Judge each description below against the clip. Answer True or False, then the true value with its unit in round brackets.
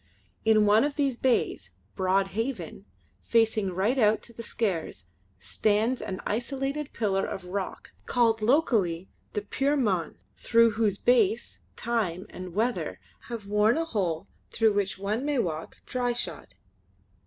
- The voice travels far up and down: False (4.0 semitones)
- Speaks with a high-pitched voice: True (220 Hz)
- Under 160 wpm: True (140 wpm)